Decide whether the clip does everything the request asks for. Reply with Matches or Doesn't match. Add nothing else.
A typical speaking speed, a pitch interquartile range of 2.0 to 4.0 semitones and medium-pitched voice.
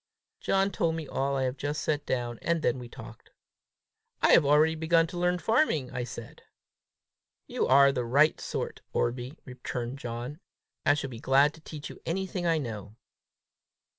Doesn't match